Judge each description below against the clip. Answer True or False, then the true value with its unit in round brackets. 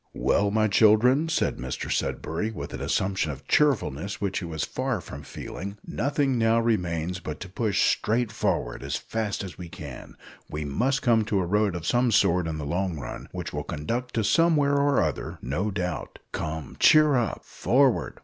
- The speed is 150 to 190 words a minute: True (185 wpm)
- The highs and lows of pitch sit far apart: True (6.4 semitones)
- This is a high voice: False (100 Hz)